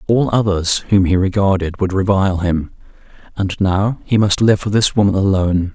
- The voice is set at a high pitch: No, very low, 95 Hz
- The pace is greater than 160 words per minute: Yes, average, 180 wpm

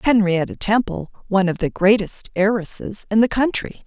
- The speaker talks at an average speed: Yes, average, 155 wpm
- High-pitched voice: Yes, high, 200 Hz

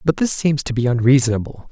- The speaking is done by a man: Yes, male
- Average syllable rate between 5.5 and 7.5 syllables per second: Yes, 6.2 syllables/s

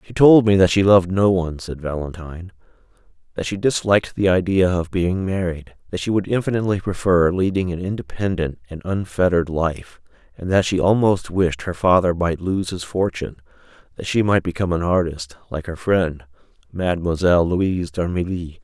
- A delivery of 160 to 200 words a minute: Yes, average, 165 wpm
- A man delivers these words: Yes, male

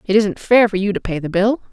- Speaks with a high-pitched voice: Yes, high, 205 Hz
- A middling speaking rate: No, fast, 315 wpm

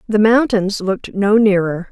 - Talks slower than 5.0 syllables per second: Yes, 4.6 syllables/s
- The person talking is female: Yes, female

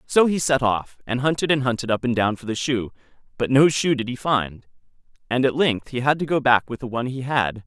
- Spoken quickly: Yes, fast, 260 wpm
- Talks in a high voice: No, low, 125 Hz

